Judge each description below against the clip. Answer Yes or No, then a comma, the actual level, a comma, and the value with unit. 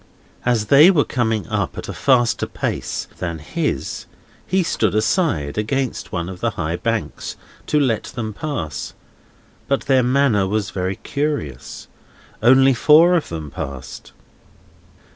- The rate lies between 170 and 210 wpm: No, average, 140 wpm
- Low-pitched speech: Yes, low, 115 Hz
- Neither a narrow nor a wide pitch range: No, wide, 7.2 semitones